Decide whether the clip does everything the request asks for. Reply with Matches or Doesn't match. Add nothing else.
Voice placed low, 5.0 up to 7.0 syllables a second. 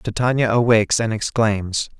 Doesn't match